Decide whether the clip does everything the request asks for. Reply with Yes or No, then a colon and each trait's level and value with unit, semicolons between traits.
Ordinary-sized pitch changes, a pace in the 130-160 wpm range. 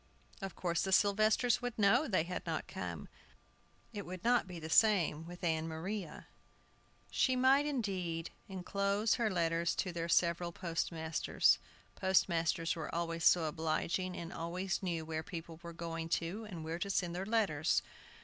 Yes: average, 3.2 semitones; average, 155 wpm